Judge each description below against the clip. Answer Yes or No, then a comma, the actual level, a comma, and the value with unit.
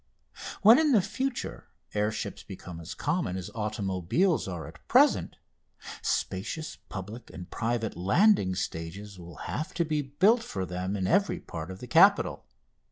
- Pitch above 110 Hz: No, low, 105 Hz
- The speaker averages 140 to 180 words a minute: Yes, average, 155 wpm